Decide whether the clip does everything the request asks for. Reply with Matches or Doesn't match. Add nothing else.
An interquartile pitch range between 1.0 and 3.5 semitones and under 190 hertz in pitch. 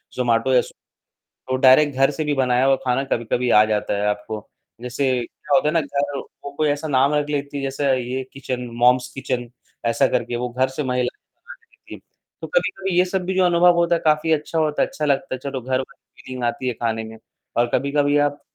Matches